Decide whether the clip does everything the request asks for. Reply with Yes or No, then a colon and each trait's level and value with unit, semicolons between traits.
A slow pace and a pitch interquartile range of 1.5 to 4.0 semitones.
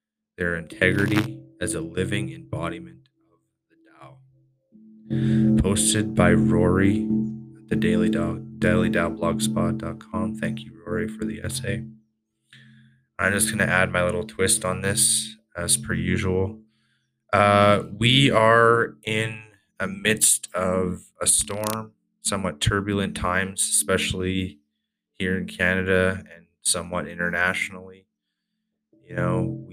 Yes: slow, 115 wpm; average, 3.1 semitones